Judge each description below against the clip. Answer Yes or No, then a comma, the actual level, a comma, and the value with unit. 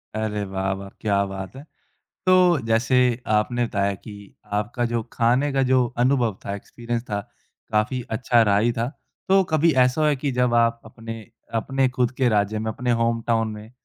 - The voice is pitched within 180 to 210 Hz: No, low, 115 Hz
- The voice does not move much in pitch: No, average, 3.1 semitones